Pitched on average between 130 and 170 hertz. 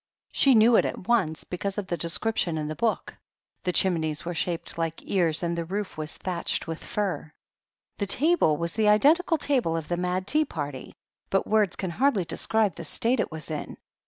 No: medium, 180 Hz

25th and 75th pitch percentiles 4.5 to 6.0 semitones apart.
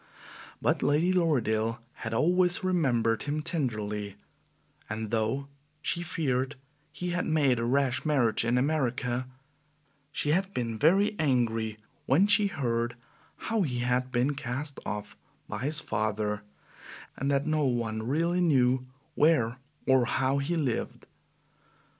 Yes: average, 5.0 semitones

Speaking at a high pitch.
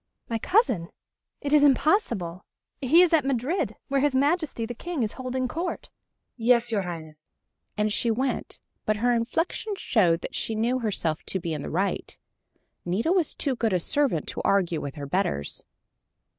Yes: high, 235 Hz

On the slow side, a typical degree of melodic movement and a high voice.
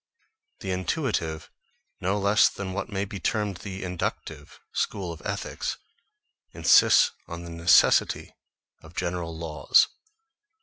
No: slow, 120 wpm; average, 3.2 semitones; very low, 95 Hz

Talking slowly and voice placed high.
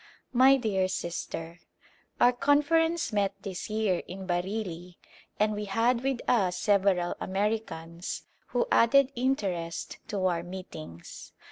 Yes: slow, 120 wpm; high, 200 Hz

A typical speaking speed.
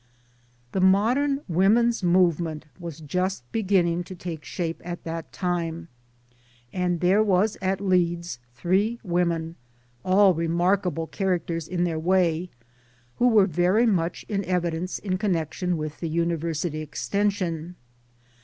No: slow, 130 wpm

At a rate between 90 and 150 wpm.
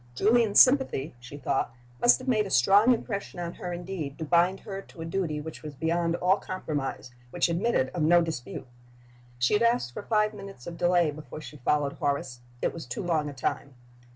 No: average, 200 wpm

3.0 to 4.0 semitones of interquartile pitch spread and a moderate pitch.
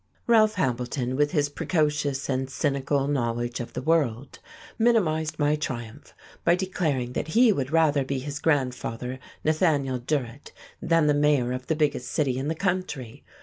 Yes: average, 3.5 semitones; medium, 145 Hz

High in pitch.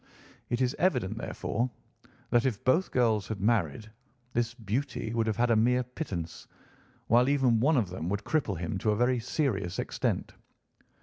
No: low, 115 Hz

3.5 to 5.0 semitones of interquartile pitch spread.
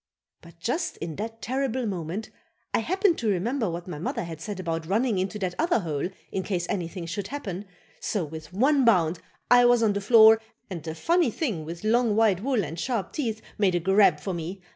No: wide, 5.4 semitones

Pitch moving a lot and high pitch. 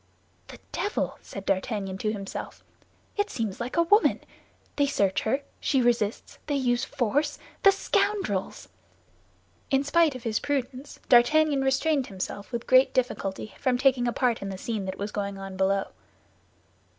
Yes: wide, 5.8 semitones; high, 245 Hz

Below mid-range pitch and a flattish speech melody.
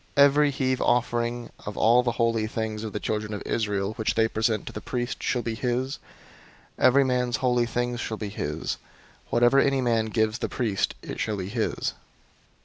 Yes: low, 120 Hz; narrow, 2.3 semitones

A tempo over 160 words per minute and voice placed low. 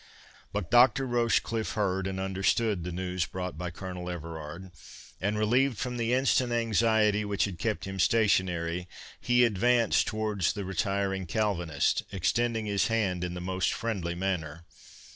No: average, 145 wpm; low, 100 Hz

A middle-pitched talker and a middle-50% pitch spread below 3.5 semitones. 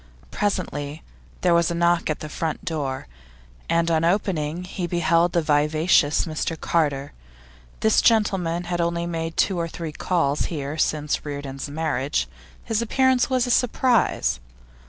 Yes: medium, 165 Hz; average, 2.8 semitones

